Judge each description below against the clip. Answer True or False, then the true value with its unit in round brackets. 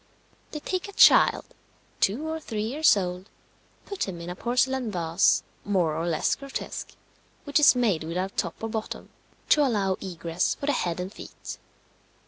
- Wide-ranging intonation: True (6.9 semitones)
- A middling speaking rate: True (165 wpm)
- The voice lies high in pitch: True (205 Hz)